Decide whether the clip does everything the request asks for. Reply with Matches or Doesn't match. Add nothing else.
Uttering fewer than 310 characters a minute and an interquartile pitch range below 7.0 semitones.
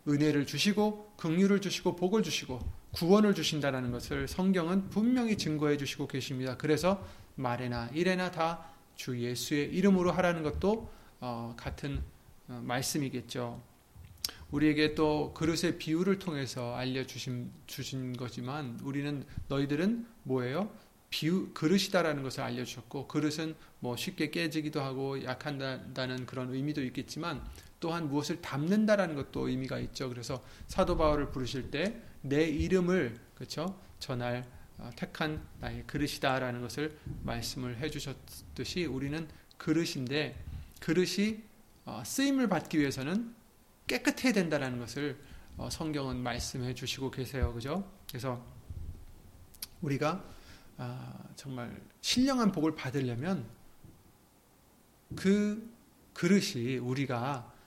Matches